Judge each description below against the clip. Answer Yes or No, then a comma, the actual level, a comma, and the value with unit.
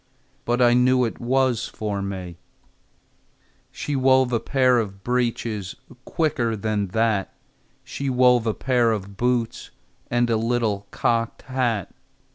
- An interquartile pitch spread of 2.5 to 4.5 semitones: Yes, average, 2.8 semitones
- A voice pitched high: No, low, 120 Hz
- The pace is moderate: No, slow, 130 wpm